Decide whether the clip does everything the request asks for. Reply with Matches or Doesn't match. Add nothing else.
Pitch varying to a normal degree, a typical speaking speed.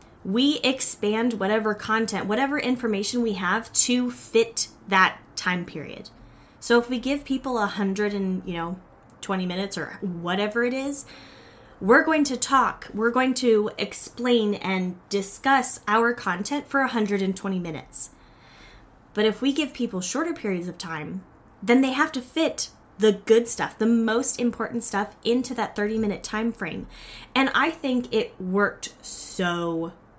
Matches